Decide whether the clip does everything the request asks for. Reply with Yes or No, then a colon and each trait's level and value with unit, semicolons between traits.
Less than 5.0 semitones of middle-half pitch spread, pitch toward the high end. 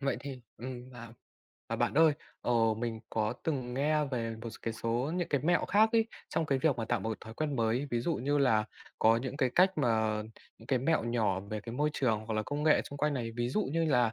No: average, 4.3 semitones; low, 125 Hz